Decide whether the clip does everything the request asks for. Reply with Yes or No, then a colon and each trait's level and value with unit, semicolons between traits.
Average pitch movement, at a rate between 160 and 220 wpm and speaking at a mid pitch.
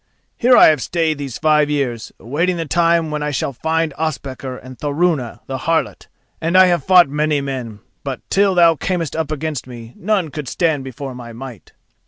Yes: average, 3.9 semitones; average, 190 wpm; medium, 150 Hz